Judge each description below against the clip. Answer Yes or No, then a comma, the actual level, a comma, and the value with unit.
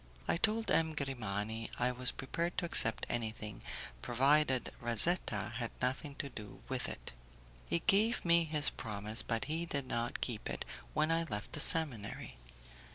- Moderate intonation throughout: No, wide, 6.3 semitones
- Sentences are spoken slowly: No, average, 160 wpm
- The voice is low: Yes, low, 130 Hz